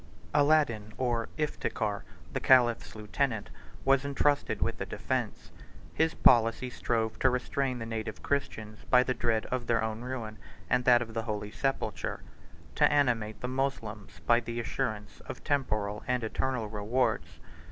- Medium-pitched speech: No, low, 120 Hz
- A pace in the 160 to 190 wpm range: No, average, 150 wpm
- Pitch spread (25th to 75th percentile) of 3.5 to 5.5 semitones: No, average, 3.1 semitones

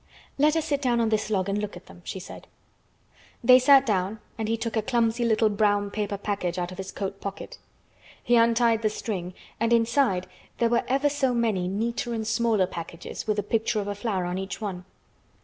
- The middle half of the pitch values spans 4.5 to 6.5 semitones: No, average, 3.1 semitones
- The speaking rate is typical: No, fast, 210 wpm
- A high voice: Yes, high, 215 Hz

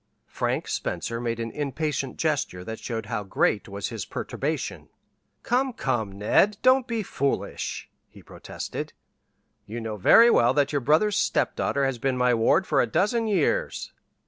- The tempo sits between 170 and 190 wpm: No, average, 155 wpm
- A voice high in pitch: No, low, 135 Hz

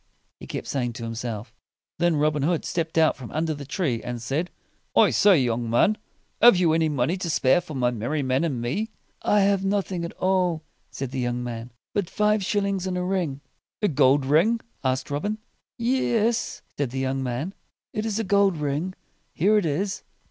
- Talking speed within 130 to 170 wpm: No, average, 195 wpm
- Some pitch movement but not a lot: No, wide, 6.6 semitones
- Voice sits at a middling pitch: Yes, medium, 160 Hz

